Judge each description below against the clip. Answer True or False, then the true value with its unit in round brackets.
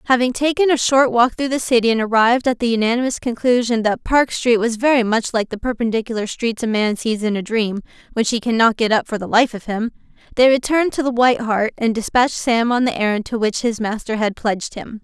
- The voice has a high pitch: True (235 Hz)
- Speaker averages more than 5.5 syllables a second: True (5.9 syllables/s)